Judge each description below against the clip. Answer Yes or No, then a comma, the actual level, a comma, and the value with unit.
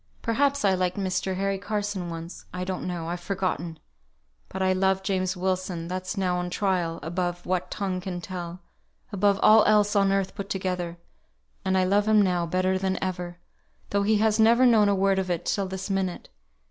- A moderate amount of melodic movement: No, narrow, 1.8 semitones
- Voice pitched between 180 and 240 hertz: Yes, high, 190 Hz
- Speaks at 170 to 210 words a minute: Yes, average, 190 wpm